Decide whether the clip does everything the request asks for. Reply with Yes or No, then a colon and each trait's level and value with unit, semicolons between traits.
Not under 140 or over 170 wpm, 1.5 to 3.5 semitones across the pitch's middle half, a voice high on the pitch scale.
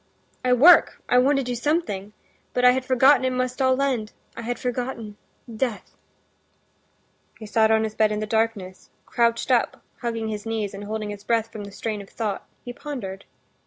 No: average, 185 wpm; average, 2.9 semitones; high, 230 Hz